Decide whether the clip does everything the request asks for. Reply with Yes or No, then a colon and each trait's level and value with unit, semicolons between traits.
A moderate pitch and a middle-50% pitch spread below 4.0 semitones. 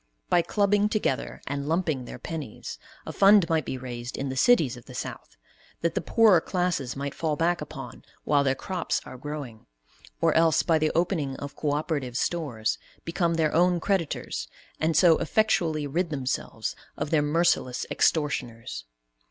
No: medium, 155 Hz; average, 4.3 semitones